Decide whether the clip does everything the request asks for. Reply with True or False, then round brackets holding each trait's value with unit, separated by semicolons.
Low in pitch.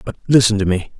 True (105 Hz)